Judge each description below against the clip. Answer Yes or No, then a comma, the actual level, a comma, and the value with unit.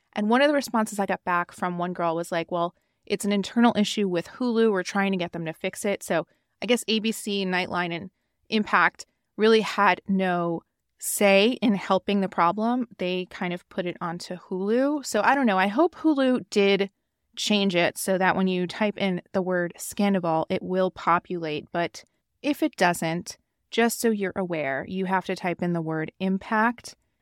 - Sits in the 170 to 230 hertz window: Yes, high, 190 Hz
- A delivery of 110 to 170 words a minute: No, average, 195 wpm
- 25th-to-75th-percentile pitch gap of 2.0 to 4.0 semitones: Yes, average, 3.5 semitones